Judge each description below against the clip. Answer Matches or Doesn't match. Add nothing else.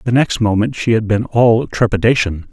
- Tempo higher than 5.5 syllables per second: Doesn't match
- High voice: Doesn't match